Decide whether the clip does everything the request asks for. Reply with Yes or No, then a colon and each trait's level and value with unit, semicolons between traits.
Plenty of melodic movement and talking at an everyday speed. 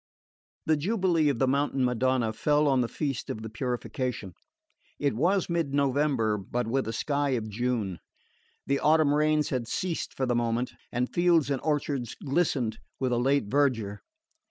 No: average, 3.7 semitones; average, 165 wpm